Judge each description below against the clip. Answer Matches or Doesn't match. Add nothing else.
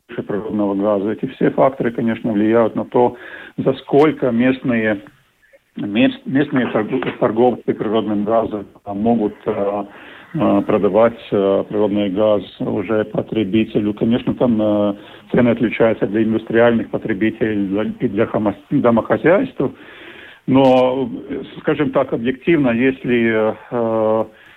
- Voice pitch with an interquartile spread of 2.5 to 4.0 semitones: Matches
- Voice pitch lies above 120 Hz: Doesn't match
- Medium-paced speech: Doesn't match